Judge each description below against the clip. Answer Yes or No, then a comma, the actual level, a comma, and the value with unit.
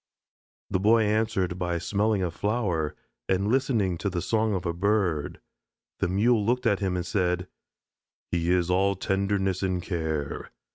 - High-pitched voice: No, very low, 95 Hz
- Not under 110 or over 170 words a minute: Yes, average, 155 wpm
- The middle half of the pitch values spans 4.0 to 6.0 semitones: No, average, 3.2 semitones